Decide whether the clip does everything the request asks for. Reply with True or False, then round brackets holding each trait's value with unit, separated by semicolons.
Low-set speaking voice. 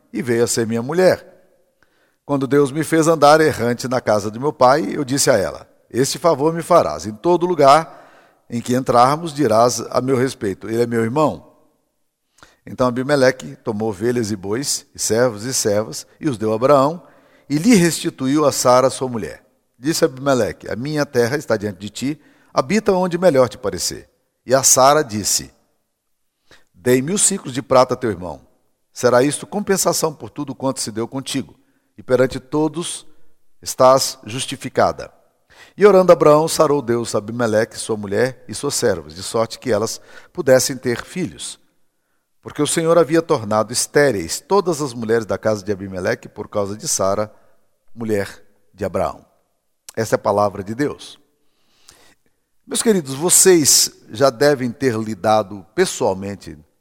True (130 Hz)